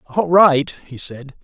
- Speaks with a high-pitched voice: No, medium, 150 Hz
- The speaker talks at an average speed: Yes, average, 165 wpm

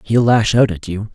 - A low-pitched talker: Yes, low, 110 Hz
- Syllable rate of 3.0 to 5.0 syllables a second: Yes, 4.8 syllables/s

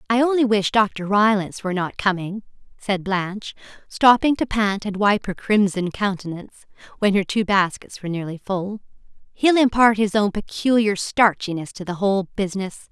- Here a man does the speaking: No, female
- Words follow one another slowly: No, average, 165 wpm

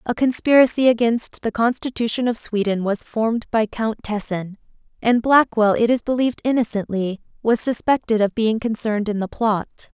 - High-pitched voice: Yes, high, 225 Hz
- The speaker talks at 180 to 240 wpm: No, average, 155 wpm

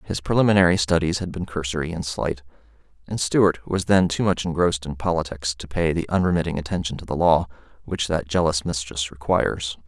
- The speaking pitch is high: No, very low, 80 Hz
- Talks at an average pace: Yes, average, 180 wpm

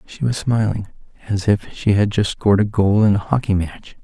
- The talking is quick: Yes, fast, 225 wpm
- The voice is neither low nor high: No, low, 105 Hz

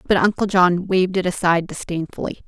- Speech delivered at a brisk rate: No, average, 170 wpm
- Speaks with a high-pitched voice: No, medium, 180 Hz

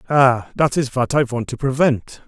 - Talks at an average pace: No, fast, 210 wpm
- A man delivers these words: Yes, male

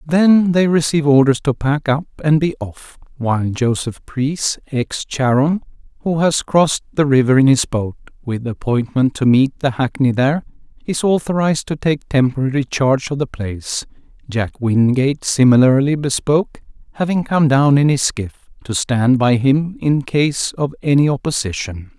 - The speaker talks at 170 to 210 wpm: No, average, 160 wpm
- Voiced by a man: Yes, male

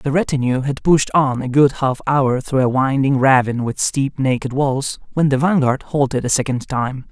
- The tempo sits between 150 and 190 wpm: No, average, 200 wpm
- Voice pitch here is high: No, low, 135 Hz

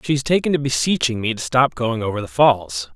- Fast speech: Yes, fast, 245 wpm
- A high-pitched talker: No, low, 120 Hz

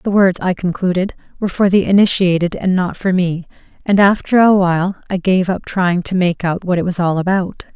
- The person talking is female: Yes, female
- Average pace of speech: No, fast, 215 wpm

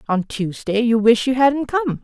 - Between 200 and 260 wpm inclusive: Yes, fast, 205 wpm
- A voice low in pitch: No, high, 240 Hz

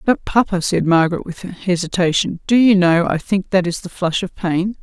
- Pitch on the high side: No, medium, 180 Hz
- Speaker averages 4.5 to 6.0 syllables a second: Yes, 5.0 syllables/s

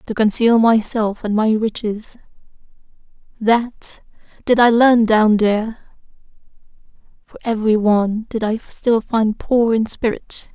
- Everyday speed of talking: No, slow, 120 wpm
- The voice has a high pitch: Yes, high, 220 Hz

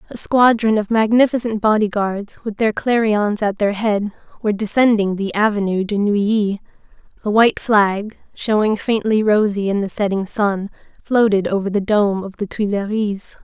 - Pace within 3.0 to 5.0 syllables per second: Yes, 4.8 syllables/s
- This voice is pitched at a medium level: No, high, 210 Hz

